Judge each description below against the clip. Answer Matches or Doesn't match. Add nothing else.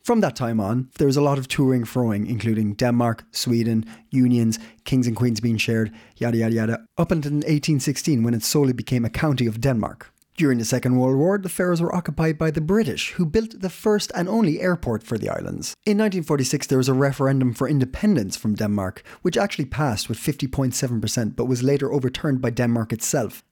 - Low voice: Matches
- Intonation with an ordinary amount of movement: Matches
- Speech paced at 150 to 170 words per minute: Doesn't match